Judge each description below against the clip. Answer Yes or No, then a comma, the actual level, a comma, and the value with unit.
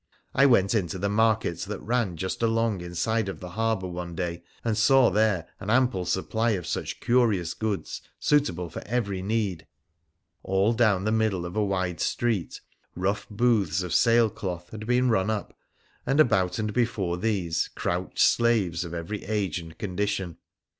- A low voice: Yes, low, 100 Hz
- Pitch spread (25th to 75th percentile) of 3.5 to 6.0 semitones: Yes, average, 3.9 semitones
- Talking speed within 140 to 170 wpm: Yes, average, 165 wpm